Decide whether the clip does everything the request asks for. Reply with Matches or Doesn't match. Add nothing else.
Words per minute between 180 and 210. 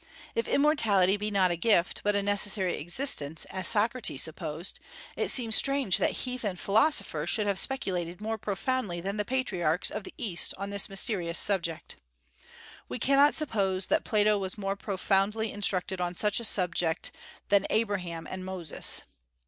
Doesn't match